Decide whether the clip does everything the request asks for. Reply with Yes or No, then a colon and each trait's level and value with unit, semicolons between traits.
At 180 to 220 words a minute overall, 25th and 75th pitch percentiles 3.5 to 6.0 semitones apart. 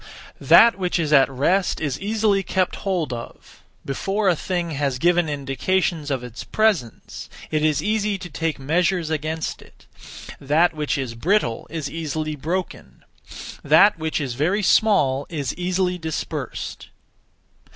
No: average, 145 wpm; average, 4.6 semitones